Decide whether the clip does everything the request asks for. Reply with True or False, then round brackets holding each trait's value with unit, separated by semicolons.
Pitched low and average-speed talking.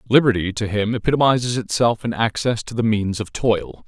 True (110 Hz; 185 wpm)